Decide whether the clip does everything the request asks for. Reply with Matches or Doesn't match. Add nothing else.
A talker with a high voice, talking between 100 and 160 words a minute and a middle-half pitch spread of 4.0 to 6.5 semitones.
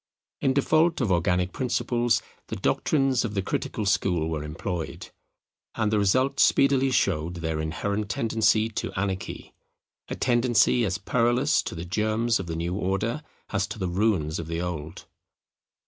Doesn't match